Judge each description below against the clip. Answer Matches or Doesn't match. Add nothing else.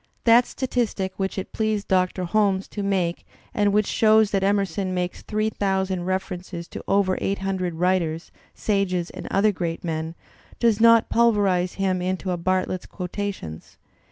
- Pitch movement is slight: Matches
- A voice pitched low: Doesn't match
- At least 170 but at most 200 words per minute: Doesn't match